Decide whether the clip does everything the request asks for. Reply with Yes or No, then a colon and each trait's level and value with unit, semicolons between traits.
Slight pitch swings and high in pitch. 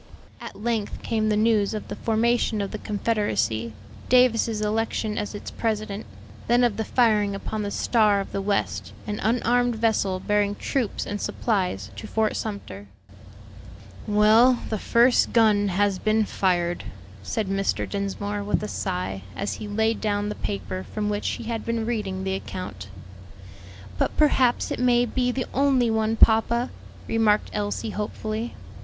Yes: narrow, 2.1 semitones; high, 215 Hz